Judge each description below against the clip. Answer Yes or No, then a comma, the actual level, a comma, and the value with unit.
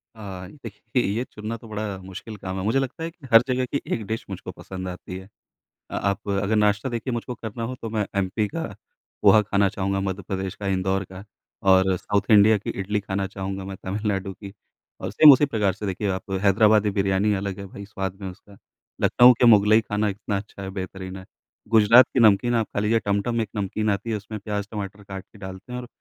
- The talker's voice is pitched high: No, low, 100 Hz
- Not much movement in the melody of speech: Yes, narrow, 2.3 semitones